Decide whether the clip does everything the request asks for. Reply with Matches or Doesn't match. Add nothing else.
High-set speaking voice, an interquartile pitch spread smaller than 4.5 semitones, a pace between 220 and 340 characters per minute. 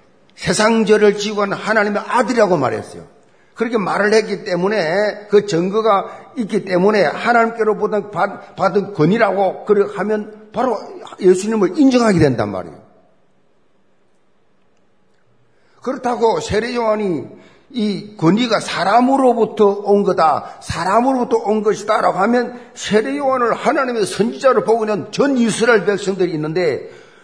Matches